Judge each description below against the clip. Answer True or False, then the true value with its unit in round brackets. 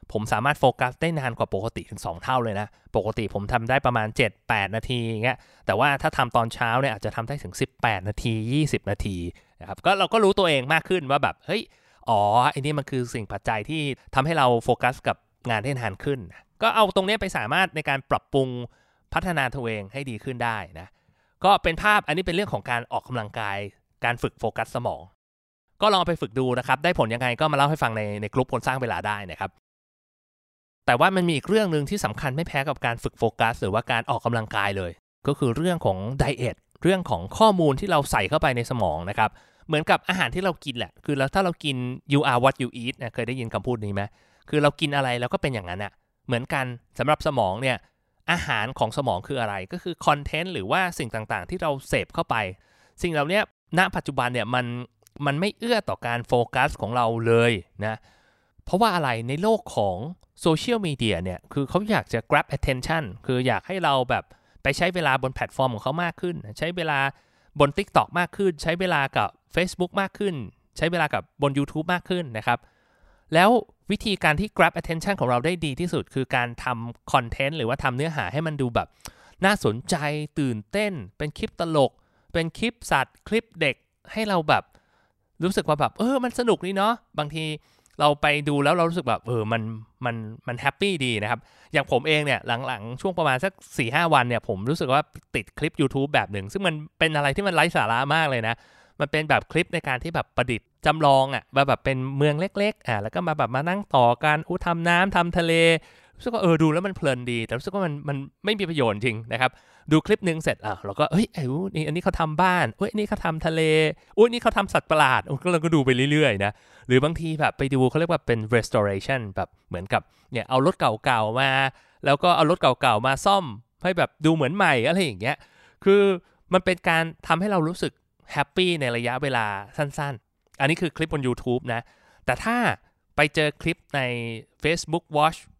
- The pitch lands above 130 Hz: True (140 Hz)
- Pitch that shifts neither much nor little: False (5.9 semitones)